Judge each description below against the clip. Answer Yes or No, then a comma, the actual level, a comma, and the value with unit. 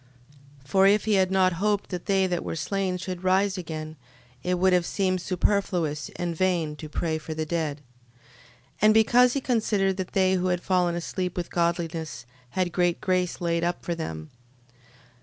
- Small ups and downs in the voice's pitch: Yes, narrow, 2.3 semitones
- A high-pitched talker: No, medium, 180 Hz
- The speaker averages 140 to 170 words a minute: No, average, 185 wpm